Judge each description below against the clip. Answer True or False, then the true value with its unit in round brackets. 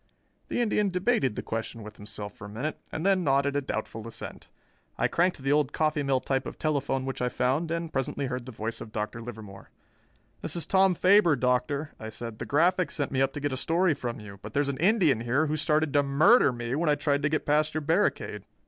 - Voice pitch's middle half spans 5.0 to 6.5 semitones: False (4.5 semitones)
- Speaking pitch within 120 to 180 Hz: True (140 Hz)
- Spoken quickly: True (230 wpm)